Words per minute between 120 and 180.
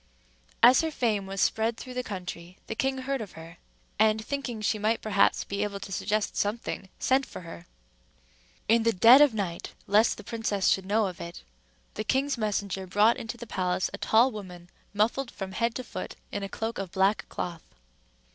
No: average, 195 wpm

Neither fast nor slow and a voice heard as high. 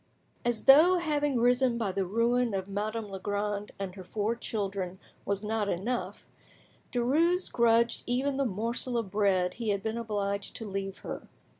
Yes: average, 160 wpm; high, 220 Hz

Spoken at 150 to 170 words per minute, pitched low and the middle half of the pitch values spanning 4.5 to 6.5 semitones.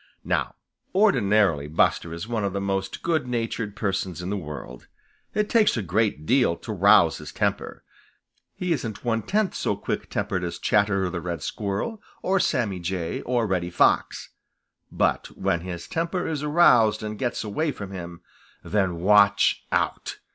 Yes: average, 160 wpm; low, 100 Hz; wide, 5.4 semitones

